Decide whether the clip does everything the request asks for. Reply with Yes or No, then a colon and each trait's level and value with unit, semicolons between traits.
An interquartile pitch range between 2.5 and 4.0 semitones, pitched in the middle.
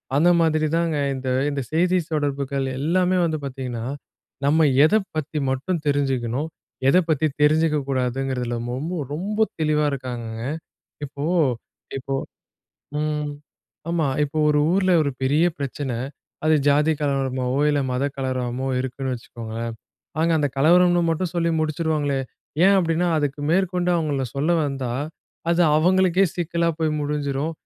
Yes: average, 3.6 semitones; medium, 150 Hz